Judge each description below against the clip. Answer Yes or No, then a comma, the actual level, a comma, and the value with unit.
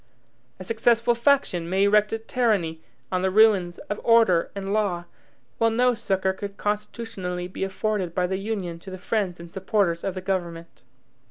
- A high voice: Yes, high, 195 Hz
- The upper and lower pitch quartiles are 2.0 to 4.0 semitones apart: Yes, average, 3.4 semitones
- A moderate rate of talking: Yes, average, 170 wpm